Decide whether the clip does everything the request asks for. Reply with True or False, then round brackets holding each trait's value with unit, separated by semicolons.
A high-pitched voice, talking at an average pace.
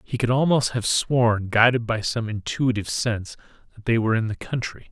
False (115 Hz; 195 wpm)